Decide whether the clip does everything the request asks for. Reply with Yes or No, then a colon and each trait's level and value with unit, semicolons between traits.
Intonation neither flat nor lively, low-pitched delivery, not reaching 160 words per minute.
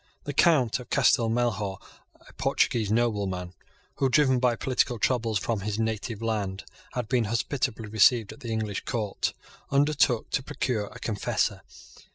Yes: average, 3.0 semitones; low, 115 Hz; average, 150 wpm